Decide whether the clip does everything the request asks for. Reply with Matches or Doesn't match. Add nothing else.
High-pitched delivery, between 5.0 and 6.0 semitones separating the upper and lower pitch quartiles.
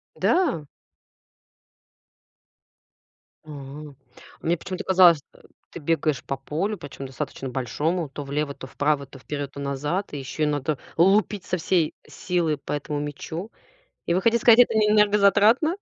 Doesn't match